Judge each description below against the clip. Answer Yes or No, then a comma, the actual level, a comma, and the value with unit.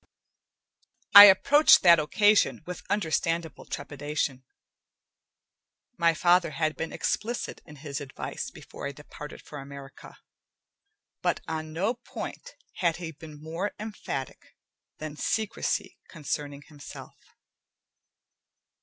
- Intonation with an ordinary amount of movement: Yes, average, 4.4 semitones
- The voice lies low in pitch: No, medium, 160 Hz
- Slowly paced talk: Yes, slow, 105 wpm